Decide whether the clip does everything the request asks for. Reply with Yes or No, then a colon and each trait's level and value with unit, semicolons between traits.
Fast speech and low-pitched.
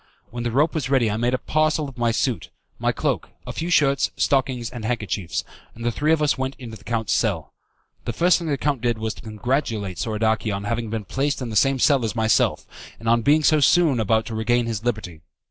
Yes: fast, 230 wpm; low, 120 Hz